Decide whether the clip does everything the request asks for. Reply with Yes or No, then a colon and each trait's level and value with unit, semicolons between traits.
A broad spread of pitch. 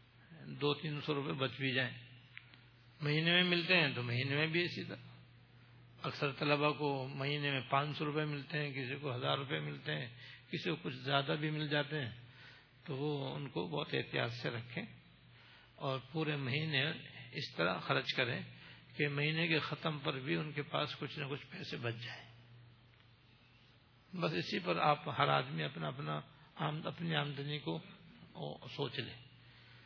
No: average, 3.5 semitones